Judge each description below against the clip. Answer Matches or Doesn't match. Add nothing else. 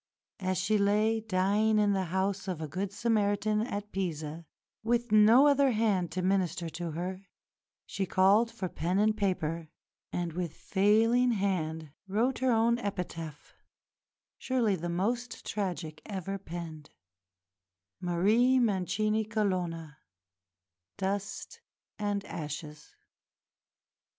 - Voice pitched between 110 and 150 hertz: Doesn't match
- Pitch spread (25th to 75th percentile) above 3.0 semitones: Matches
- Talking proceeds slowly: Matches